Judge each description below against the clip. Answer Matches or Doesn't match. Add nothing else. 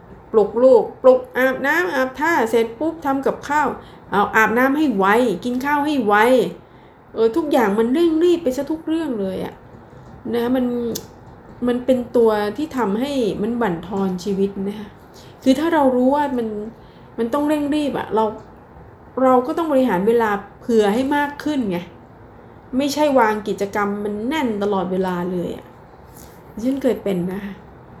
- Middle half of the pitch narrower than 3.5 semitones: Doesn't match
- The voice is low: Doesn't match